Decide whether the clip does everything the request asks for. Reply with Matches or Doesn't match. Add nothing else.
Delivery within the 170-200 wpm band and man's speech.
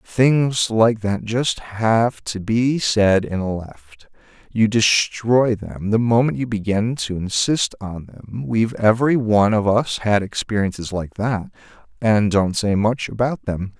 Doesn't match